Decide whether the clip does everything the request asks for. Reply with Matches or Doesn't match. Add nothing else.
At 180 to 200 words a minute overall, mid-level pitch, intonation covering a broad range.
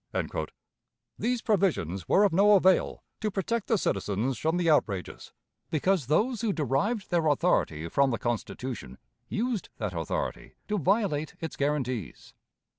Doesn't match